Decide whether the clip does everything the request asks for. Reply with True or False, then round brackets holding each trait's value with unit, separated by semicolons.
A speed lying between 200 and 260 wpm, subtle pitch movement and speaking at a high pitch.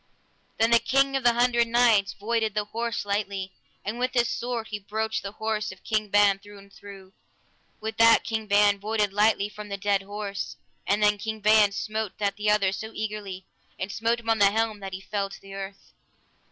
True (205 wpm; 1.9 semitones; 210 Hz)